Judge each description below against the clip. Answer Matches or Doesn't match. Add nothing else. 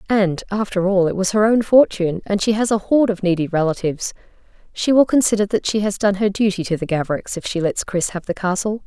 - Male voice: Doesn't match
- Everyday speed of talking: Doesn't match